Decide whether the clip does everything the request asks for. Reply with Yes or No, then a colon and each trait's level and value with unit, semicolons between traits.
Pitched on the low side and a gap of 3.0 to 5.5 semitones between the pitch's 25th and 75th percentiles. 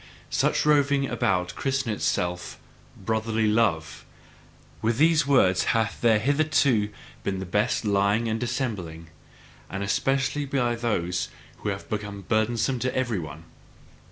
Yes: low, 110 Hz; average, 4.7 semitones